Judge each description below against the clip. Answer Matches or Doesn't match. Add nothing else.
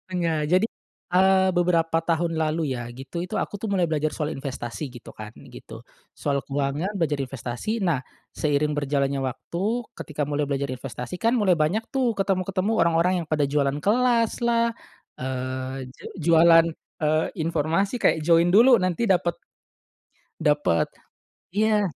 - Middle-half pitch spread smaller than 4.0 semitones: Doesn't match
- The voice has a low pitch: Doesn't match